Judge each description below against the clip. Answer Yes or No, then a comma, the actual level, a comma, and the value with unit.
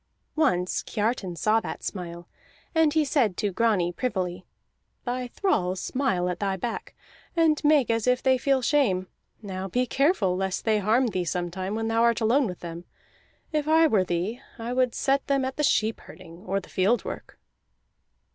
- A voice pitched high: Yes, high, 225 Hz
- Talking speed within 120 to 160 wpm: No, average, 175 wpm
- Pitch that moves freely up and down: Yes, wide, 6.0 semitones